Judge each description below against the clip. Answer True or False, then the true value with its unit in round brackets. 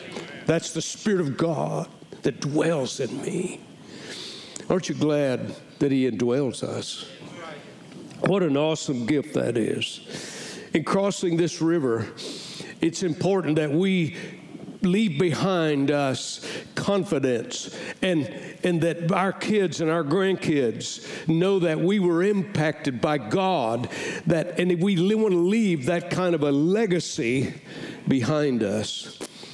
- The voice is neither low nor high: True (170 Hz)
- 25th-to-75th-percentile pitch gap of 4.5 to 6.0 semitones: False (3.8 semitones)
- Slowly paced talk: True (130 wpm)